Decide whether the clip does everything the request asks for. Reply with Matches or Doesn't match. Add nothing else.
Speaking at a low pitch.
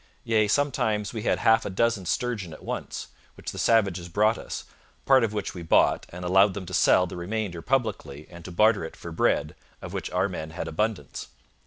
Matches